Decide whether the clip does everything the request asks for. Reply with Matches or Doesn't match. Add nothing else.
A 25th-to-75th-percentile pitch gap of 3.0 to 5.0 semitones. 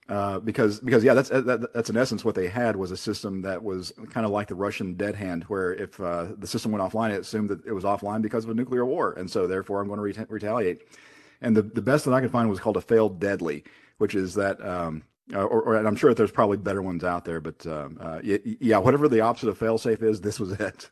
Doesn't match